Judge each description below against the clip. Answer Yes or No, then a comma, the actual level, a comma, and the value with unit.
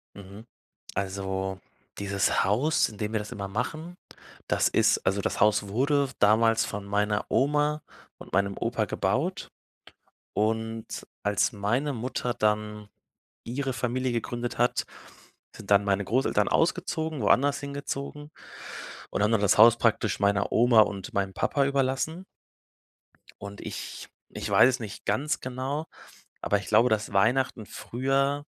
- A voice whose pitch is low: Yes, low, 115 Hz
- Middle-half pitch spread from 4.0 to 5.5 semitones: Yes, average, 4.8 semitones